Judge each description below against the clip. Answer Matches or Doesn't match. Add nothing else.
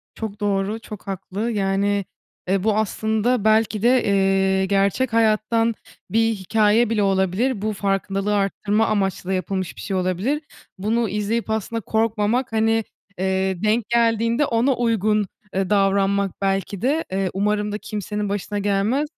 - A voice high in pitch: Matches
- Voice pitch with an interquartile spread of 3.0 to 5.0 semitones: Doesn't match